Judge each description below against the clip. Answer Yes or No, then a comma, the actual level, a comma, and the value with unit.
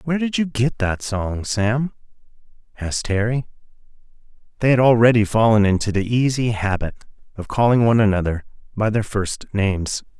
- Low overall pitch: Yes, low, 110 Hz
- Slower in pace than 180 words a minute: Yes, average, 140 wpm